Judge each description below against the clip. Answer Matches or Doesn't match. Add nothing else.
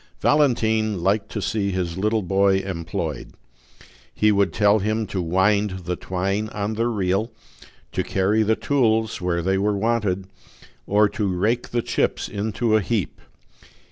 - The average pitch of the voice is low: Matches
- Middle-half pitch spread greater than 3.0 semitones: Doesn't match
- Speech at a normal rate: Matches